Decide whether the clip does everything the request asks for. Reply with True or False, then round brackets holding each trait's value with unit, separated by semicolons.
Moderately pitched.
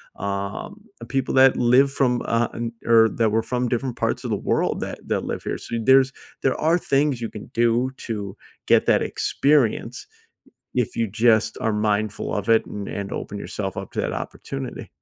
False (115 Hz)